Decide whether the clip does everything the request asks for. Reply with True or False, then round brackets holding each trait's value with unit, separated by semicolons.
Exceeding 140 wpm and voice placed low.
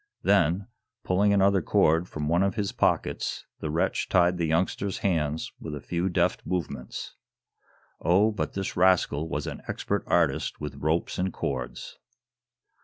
True (150 wpm; 85 Hz)